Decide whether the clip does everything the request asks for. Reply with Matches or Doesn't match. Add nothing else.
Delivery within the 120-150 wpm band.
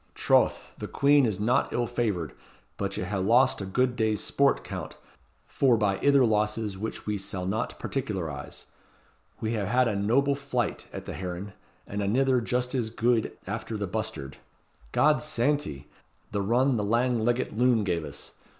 Doesn't match